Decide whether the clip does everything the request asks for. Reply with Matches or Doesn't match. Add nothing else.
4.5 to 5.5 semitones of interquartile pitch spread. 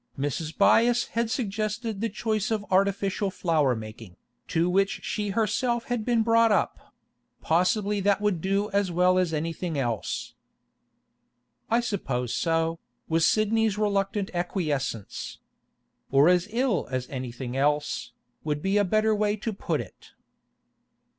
Matches